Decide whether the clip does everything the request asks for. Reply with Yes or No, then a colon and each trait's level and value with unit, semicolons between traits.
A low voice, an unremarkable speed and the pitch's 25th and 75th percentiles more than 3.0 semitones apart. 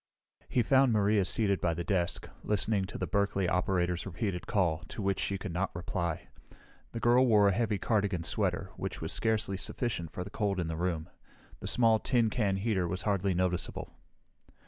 Yes: low, 100 Hz; average, 185 wpm; average, 3.4 semitones